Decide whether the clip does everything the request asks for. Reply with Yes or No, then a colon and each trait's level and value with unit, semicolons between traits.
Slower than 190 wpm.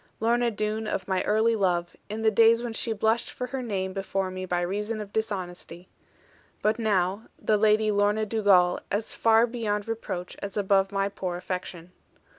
Yes: average, 175 wpm